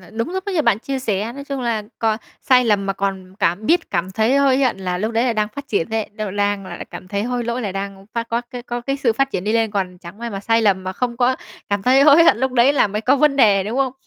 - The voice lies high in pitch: Yes, high, 225 Hz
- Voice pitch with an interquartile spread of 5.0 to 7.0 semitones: No, average, 4.4 semitones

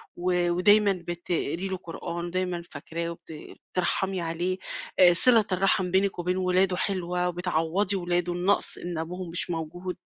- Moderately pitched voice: Yes, medium, 180 Hz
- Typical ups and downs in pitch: No, narrow, 1.4 semitones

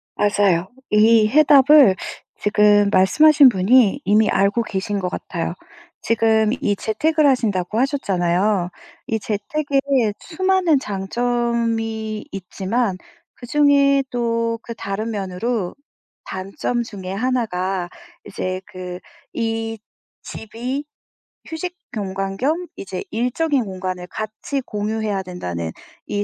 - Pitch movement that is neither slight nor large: Yes, average, 4.5 semitones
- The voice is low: No, high, 220 Hz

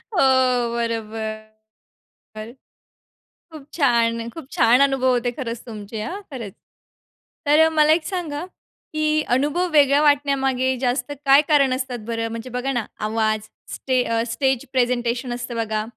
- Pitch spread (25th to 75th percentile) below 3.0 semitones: No, average, 3.3 semitones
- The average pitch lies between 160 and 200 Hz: No, very high, 250 Hz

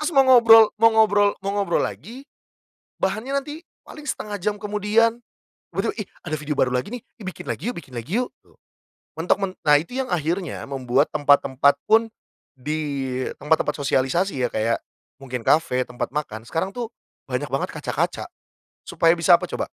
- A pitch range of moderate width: No, wide, 7.9 semitones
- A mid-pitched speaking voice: Yes, medium, 175 Hz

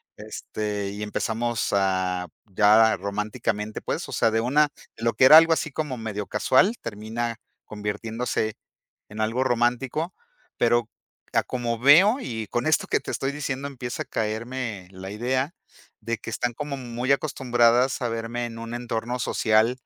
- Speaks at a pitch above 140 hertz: No, low, 115 Hz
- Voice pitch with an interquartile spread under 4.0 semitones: Yes, average, 3.1 semitones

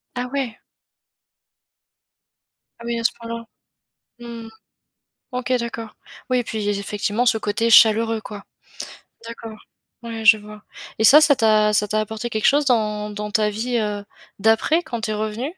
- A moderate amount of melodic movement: No, narrow, 2.0 semitones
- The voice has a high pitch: Yes, high, 225 Hz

